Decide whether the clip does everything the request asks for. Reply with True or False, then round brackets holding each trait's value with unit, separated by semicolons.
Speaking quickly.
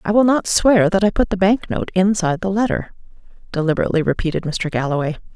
False (190 wpm)